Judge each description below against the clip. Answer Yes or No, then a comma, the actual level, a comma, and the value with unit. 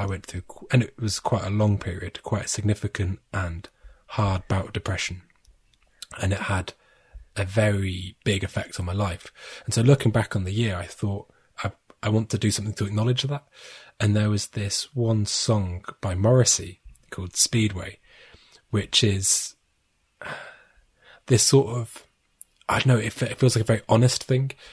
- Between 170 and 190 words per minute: Yes, average, 175 wpm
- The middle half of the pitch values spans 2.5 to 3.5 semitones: Yes, average, 3.0 semitones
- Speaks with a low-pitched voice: Yes, low, 105 Hz